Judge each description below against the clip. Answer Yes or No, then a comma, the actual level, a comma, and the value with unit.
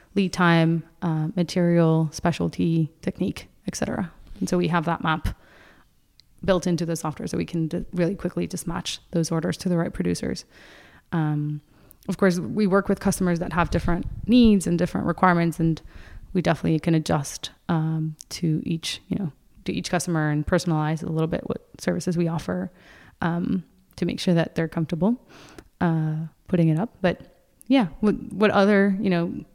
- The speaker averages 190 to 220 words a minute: No, average, 175 wpm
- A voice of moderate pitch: Yes, medium, 170 Hz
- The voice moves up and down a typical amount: No, narrow, 2.3 semitones